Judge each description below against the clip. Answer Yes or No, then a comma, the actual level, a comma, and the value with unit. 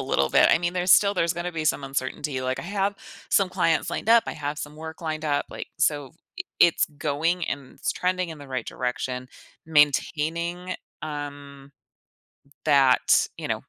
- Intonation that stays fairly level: No, average, 3.7 semitones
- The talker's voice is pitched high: No, medium, 155 Hz